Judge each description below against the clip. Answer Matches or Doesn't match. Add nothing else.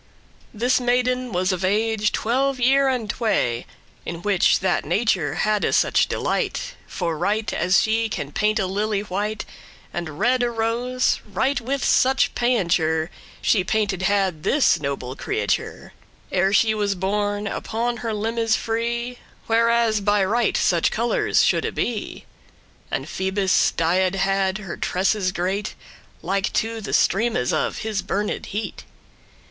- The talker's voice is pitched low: Doesn't match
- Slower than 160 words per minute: Matches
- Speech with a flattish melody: Doesn't match